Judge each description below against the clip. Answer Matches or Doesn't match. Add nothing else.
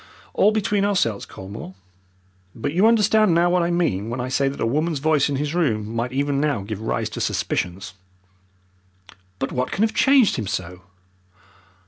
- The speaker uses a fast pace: Doesn't match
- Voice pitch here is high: Doesn't match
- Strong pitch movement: Matches